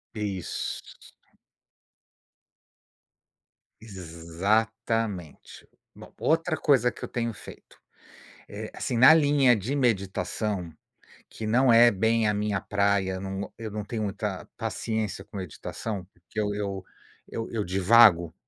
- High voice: No, low, 105 Hz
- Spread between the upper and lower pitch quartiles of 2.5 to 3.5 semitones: Yes, average, 3.2 semitones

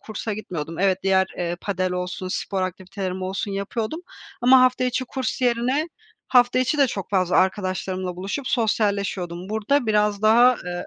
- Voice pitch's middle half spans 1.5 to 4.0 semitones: No, average, 4.6 semitones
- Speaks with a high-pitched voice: Yes, high, 200 Hz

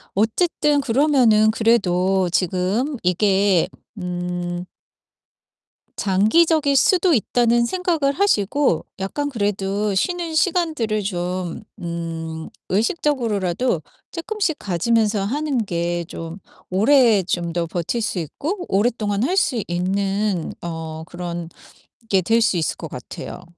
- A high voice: Yes, high, 205 Hz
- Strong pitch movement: Yes, wide, 7.1 semitones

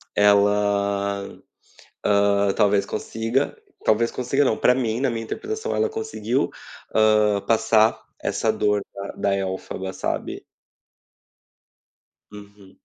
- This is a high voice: No, low, 105 Hz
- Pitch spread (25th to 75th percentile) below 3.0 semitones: Yes, narrow, 2.5 semitones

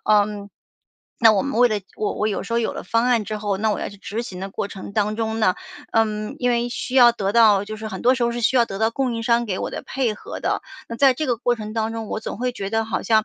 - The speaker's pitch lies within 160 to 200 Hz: No, high, 225 Hz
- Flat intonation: Yes, narrow, 2.1 semitones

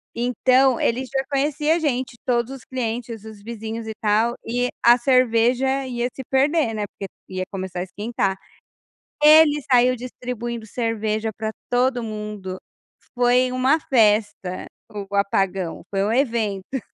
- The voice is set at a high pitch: Yes, high, 235 Hz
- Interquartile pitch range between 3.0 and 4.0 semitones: Yes, average, 3.3 semitones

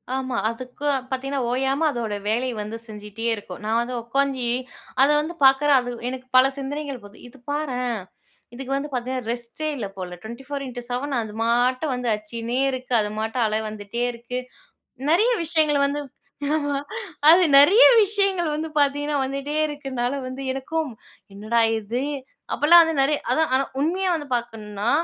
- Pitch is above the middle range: Yes, very high, 260 Hz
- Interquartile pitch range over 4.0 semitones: No, average, 3.7 semitones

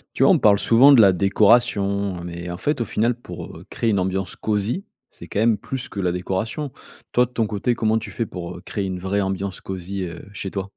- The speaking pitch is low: Yes, low, 100 Hz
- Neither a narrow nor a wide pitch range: Yes, average, 3.3 semitones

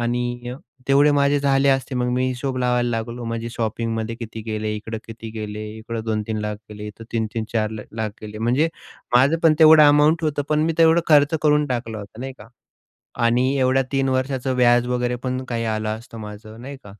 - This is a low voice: Yes, low, 120 Hz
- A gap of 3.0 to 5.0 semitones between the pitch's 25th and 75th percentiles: Yes, average, 3.4 semitones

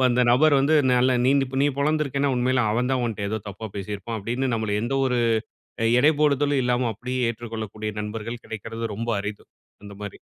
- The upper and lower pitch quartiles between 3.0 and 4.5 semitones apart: Yes, average, 3.3 semitones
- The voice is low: Yes, low, 120 Hz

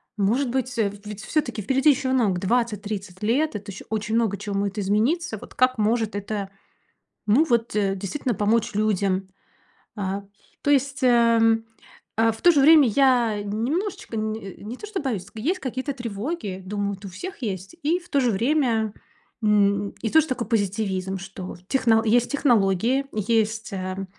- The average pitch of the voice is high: Yes, high, 220 Hz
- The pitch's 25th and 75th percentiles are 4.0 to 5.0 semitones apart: Yes, average, 4.3 semitones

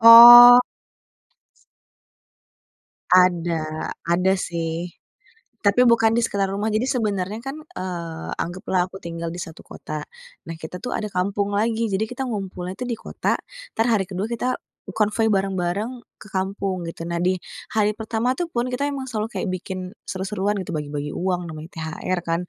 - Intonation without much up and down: No, average, 4.2 semitones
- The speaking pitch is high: Yes, high, 195 Hz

